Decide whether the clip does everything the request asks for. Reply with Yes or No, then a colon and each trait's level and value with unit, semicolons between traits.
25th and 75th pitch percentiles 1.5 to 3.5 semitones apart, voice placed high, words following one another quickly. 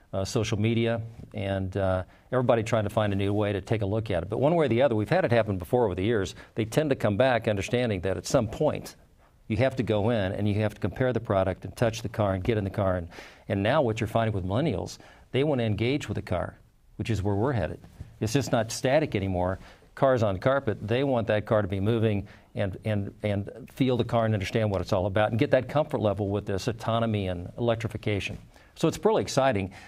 No: average, 2.8 semitones; low, 110 Hz; fast, 250 wpm